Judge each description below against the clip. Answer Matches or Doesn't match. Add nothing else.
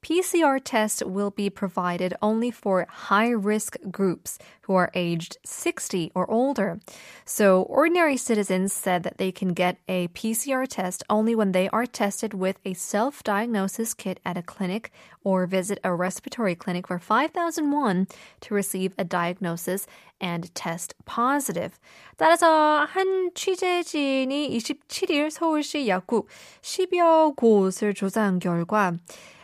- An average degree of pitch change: Doesn't match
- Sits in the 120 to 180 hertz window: Doesn't match